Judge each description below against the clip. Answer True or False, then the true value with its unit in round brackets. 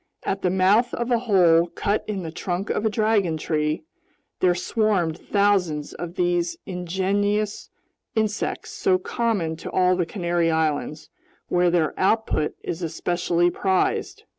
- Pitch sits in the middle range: True (180 Hz)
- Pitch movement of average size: True (3.3 semitones)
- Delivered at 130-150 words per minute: True (140 wpm)